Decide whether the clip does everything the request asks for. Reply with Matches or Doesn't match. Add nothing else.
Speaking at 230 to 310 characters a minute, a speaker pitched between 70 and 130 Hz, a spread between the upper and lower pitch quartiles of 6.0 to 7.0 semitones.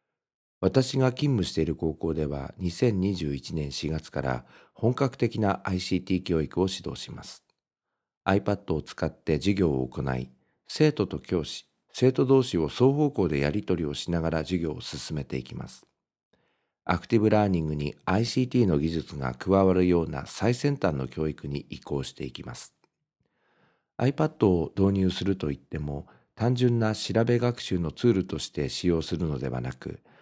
Matches